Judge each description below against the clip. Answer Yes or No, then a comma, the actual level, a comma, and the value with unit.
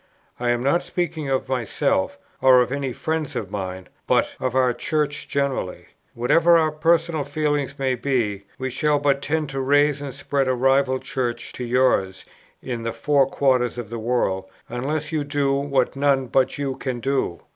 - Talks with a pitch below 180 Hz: Yes, low, 135 Hz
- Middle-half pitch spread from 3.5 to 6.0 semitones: No, average, 2.8 semitones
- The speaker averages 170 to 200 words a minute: Yes, average, 180 wpm